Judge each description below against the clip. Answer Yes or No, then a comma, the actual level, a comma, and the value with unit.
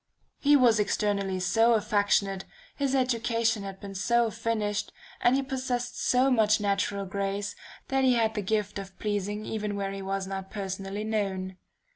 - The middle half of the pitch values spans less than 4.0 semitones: Yes, average, 2.9 semitones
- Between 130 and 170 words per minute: Yes, average, 160 wpm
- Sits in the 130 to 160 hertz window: No, high, 210 Hz